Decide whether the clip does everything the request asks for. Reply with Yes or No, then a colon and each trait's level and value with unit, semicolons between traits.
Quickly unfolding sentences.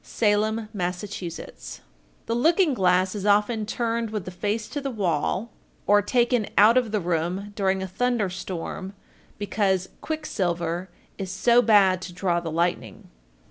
No: average, 155 wpm